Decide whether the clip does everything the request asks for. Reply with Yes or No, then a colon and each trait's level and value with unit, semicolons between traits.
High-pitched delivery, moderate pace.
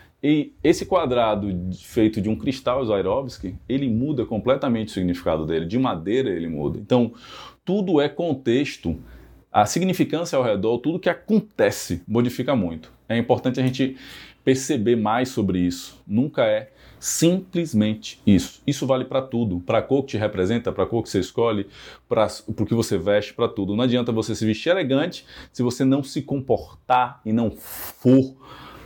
No: low, 120 Hz; average, 165 wpm